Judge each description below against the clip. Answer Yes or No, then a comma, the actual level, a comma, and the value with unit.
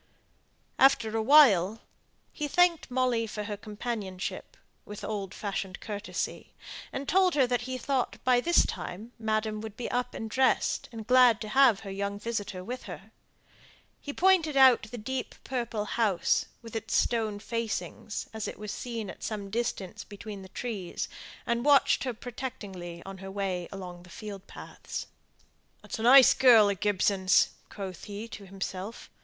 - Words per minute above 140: Yes, average, 160 wpm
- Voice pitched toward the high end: Yes, high, 220 Hz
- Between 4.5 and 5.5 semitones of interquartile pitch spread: No, average, 3.8 semitones